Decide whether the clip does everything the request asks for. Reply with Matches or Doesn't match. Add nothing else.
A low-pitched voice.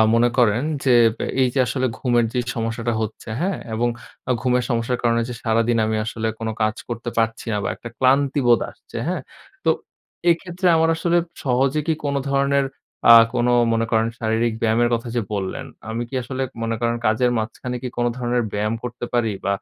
Matches